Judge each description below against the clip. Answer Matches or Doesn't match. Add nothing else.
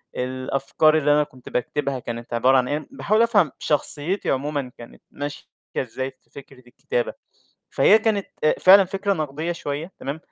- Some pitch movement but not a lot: Doesn't match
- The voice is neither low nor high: Matches